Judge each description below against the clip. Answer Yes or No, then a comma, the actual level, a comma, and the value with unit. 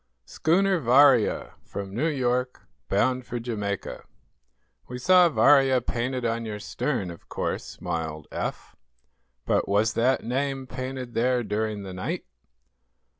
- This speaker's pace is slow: Yes, slow, 125 wpm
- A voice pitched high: No, low, 125 Hz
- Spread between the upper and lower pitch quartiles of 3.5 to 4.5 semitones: Yes, average, 4.0 semitones